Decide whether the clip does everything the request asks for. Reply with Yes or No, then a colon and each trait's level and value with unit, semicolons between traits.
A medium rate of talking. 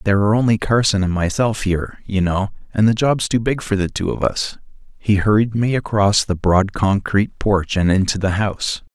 No: fast, 210 wpm